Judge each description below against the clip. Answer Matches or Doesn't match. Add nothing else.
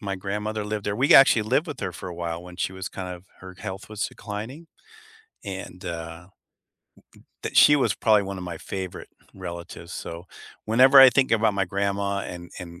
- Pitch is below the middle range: Matches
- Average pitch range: Matches